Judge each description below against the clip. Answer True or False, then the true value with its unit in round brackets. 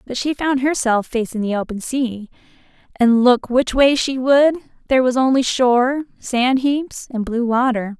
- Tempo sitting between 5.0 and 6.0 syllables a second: False (4.5 syllables/s)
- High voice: True (250 Hz)